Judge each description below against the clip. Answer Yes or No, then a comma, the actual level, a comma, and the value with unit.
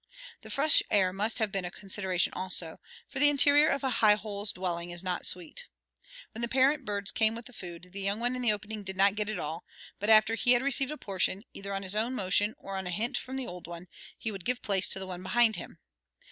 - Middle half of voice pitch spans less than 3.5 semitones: No, average, 4.2 semitones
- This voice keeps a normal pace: No, fast, 245 wpm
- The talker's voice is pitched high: Yes, high, 205 Hz